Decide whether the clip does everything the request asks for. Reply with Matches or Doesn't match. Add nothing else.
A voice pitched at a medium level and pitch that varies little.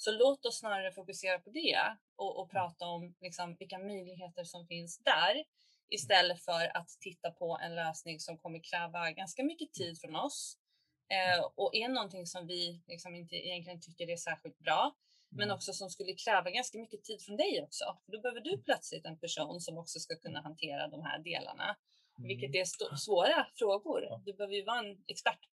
Doesn't match